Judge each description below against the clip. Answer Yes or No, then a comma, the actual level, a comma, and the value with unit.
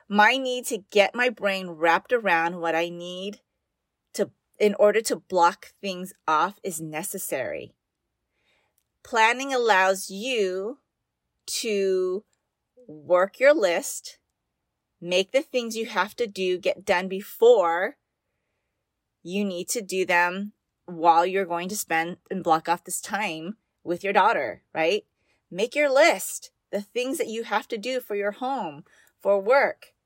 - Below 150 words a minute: Yes, average, 140 wpm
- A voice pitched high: Yes, high, 200 Hz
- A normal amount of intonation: Yes, average, 4.7 semitones